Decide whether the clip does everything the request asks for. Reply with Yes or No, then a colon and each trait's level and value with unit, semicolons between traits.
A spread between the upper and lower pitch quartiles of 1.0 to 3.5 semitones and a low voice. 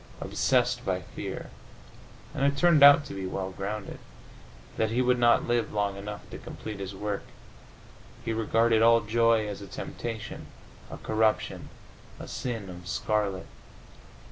Yes: average, 2.7 semitones; low, 110 Hz